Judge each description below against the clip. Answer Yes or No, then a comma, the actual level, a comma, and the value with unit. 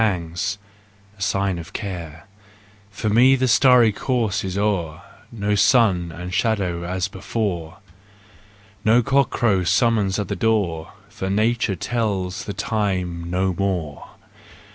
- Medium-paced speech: No, slow, 125 wpm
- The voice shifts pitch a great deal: No, average, 3.8 semitones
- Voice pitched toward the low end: Yes, low, 100 Hz